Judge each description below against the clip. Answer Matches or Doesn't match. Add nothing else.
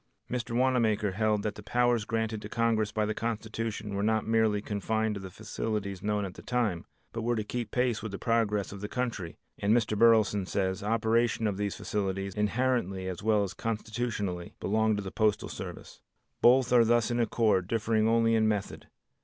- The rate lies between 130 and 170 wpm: Doesn't match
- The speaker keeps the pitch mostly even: Matches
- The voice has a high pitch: Doesn't match